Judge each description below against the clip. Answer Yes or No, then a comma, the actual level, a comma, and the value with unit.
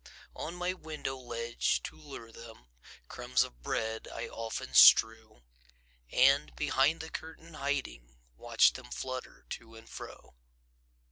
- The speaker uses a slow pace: Yes, slow, 130 wpm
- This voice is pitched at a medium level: No, low, 120 Hz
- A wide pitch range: No, average, 4.7 semitones